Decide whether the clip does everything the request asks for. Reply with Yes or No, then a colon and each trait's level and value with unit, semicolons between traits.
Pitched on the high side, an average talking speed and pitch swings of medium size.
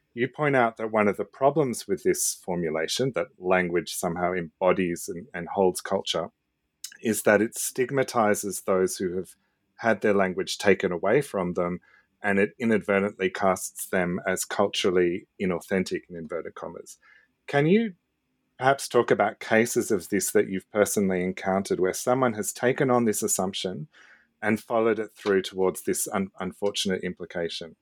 No: low, 100 Hz; average, 155 wpm; average, 4.1 semitones